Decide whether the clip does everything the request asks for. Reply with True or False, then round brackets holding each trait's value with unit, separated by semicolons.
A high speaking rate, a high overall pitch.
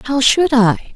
False (190 wpm; 250 Hz)